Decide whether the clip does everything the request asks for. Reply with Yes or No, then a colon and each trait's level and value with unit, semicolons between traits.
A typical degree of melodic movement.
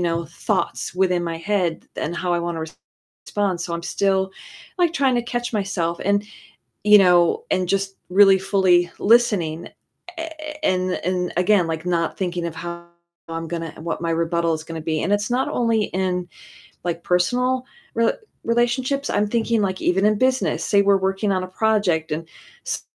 Yes: average, 3.5 semitones